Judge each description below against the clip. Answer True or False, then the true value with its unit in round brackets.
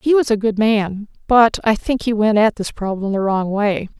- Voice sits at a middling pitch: False (215 Hz)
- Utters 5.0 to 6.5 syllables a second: False (4.7 syllables/s)